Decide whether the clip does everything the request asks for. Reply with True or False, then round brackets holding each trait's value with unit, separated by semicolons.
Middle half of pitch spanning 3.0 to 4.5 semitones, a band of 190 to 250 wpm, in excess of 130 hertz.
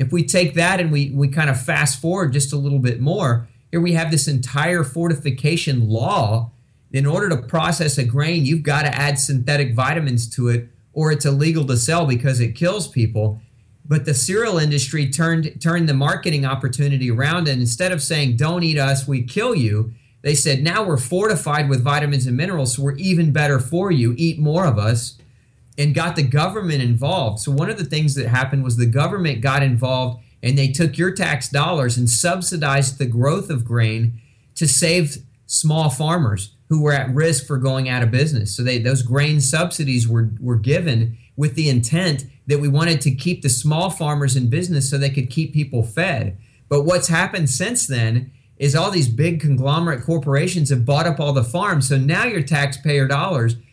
True (4.1 semitones; 195 wpm; 140 Hz)